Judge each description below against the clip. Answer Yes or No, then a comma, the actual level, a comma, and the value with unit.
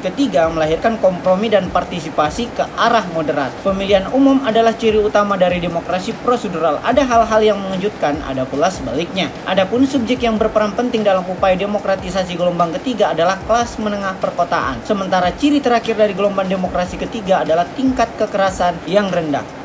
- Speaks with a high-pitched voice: Yes, high, 200 Hz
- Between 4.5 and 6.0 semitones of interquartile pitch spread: No, average, 4.0 semitones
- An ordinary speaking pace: No, fast, 150 wpm